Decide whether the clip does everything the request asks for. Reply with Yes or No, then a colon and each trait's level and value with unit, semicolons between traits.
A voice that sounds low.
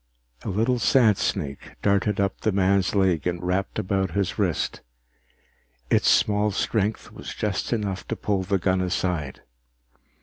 Yes: low, 100 Hz